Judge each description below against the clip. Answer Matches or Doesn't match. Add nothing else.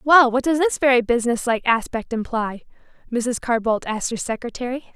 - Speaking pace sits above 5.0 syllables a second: Matches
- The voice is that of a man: Doesn't match